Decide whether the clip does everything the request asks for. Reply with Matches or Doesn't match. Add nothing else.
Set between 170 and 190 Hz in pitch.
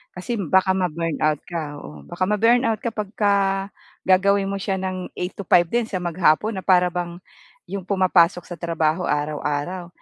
Matches